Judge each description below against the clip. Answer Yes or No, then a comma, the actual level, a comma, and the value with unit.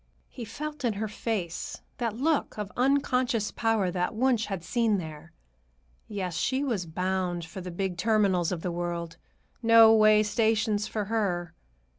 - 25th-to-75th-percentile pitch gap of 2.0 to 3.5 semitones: No, average, 4.3 semitones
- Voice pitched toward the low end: No, high, 210 Hz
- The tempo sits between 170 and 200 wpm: No, average, 155 wpm